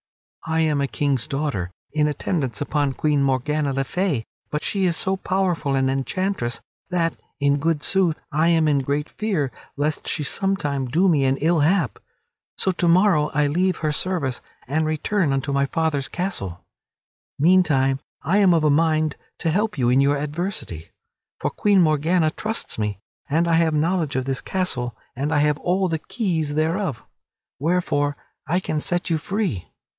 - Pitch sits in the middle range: Yes, medium, 155 Hz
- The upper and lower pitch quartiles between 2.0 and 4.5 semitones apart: Yes, average, 4.1 semitones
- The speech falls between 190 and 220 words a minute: No, average, 175 wpm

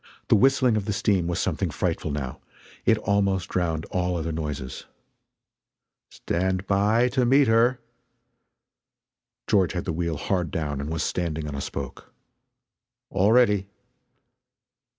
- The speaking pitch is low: Yes, very low, 95 Hz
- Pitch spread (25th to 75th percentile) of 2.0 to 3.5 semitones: No, average, 4.6 semitones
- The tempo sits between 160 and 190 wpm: No, slow, 135 wpm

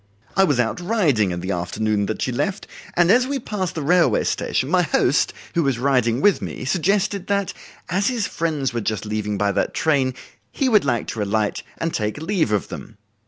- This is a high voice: No, medium, 140 Hz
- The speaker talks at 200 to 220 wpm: Yes, fast, 205 wpm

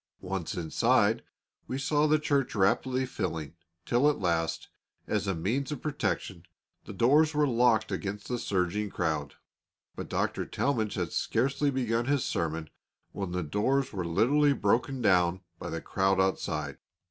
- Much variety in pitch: Yes, wide, 6.9 semitones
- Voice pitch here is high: No, low, 105 Hz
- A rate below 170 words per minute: Yes, average, 150 wpm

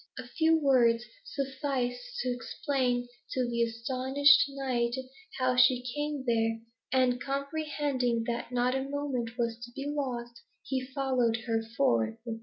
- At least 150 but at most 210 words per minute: No, slow, 135 wpm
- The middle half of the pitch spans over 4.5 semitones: No, narrow, 2.6 semitones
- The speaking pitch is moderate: No, very high, 255 Hz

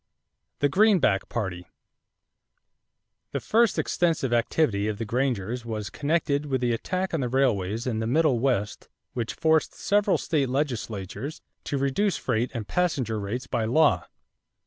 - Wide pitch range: Yes, wide, 5.8 semitones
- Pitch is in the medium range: No, low, 125 Hz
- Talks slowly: No, average, 145 wpm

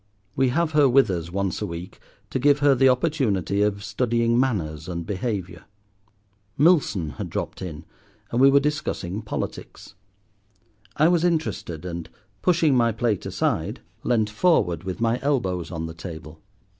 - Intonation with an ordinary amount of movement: No, wide, 7.4 semitones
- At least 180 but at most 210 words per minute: No, average, 155 wpm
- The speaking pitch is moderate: No, low, 110 Hz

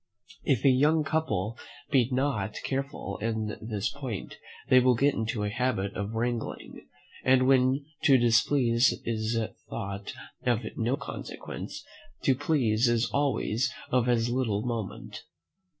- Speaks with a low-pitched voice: Yes, low, 120 Hz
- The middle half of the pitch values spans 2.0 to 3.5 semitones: Yes, average, 3.2 semitones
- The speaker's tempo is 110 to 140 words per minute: Yes, slow, 135 wpm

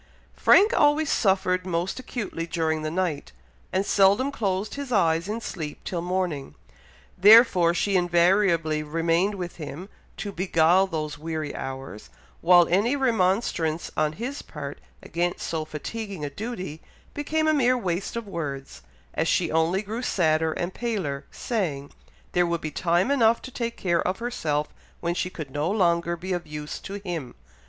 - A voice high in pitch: No, medium, 175 Hz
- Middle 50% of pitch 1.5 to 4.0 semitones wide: No, average, 4.5 semitones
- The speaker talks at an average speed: Yes, average, 160 wpm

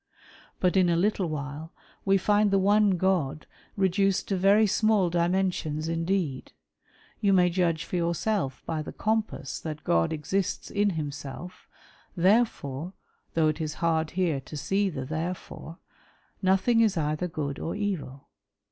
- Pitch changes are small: No, average, 4.0 semitones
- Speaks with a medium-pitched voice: Yes, medium, 175 Hz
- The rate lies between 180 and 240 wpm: No, average, 165 wpm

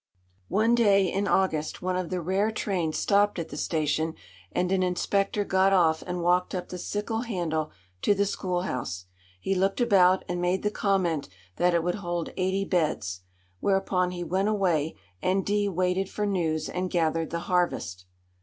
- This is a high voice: No, medium, 180 Hz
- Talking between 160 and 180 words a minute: Yes, average, 175 wpm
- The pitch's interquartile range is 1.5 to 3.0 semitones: Yes, narrow, 2.6 semitones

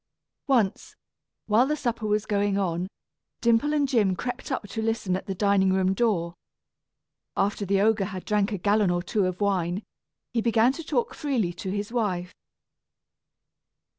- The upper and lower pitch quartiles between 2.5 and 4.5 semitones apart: Yes, average, 3.4 semitones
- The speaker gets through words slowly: No, average, 165 wpm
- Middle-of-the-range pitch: No, high, 205 Hz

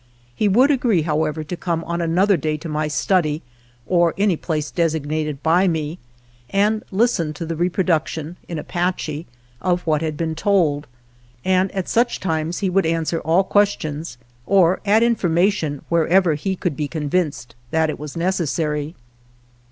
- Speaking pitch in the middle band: Yes, medium, 165 Hz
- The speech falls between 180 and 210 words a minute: No, average, 150 wpm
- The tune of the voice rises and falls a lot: No, average, 3.4 semitones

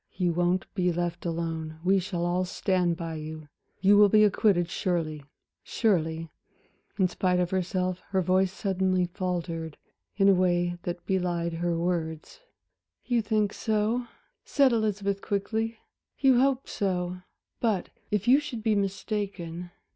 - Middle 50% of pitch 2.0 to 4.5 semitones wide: Yes, average, 2.9 semitones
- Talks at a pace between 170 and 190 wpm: No, average, 140 wpm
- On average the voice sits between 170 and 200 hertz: Yes, medium, 185 Hz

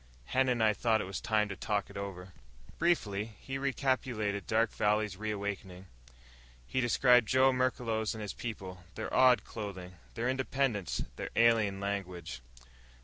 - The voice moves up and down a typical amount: Yes, average, 3.9 semitones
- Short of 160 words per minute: Yes, average, 145 wpm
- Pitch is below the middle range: Yes, low, 110 Hz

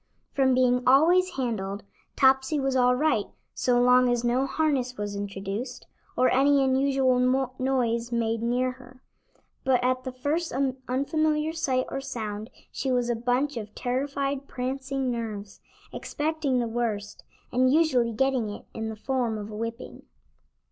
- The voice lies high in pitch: Yes, very high, 255 Hz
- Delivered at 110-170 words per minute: Yes, average, 150 wpm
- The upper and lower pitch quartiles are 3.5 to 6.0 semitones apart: No, narrow, 2.5 semitones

